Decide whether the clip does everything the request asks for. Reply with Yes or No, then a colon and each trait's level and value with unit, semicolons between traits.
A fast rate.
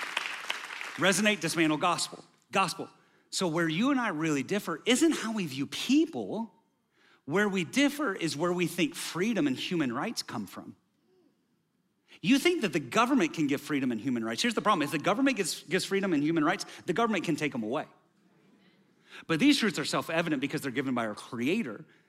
No: average, 190 wpm